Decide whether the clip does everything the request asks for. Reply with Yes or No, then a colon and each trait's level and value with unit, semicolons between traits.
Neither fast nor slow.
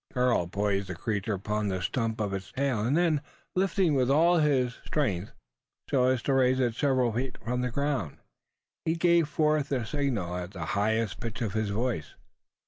Yes: average, 185 wpm